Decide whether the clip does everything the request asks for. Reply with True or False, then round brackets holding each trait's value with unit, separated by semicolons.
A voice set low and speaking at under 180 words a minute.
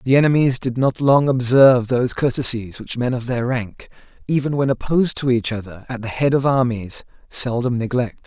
False (125 Hz; 190 wpm)